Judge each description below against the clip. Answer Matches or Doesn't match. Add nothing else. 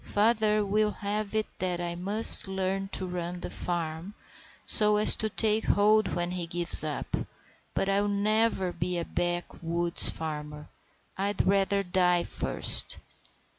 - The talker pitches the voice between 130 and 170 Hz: Doesn't match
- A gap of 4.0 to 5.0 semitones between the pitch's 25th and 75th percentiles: Doesn't match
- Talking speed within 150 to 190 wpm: Doesn't match